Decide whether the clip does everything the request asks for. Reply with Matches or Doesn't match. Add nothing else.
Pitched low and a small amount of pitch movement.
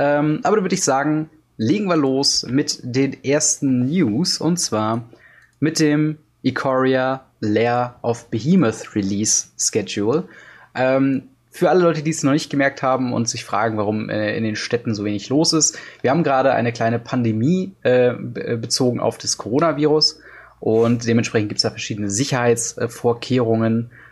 Doesn't match